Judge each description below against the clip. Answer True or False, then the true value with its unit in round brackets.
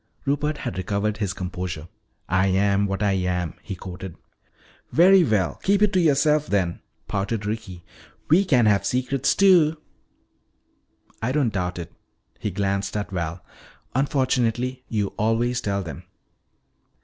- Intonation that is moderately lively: False (6.0 semitones)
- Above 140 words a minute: False (135 wpm)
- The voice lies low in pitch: True (105 Hz)